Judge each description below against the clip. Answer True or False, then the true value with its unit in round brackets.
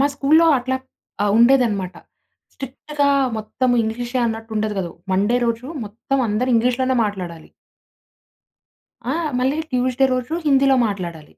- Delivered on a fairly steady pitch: False (4.1 semitones)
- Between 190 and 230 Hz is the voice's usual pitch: False (245 Hz)